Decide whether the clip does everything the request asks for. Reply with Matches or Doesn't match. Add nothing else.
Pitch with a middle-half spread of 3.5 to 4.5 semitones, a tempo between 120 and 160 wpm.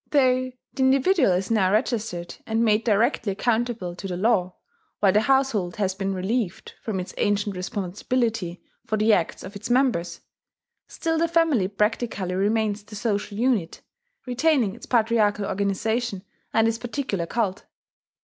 Matches